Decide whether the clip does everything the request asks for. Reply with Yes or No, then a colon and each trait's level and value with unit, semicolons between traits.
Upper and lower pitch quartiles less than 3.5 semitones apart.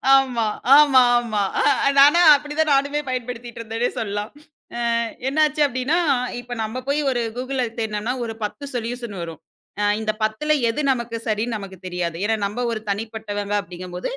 No: average, 4.0 semitones